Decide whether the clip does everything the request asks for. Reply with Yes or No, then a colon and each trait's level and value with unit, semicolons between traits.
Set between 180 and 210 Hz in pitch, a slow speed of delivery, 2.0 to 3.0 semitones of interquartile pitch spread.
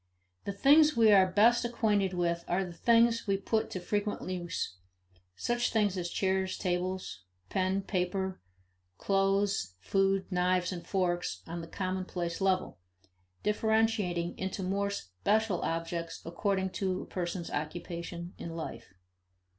Yes: high, 190 Hz; slow, 130 wpm; narrow, 2.6 semitones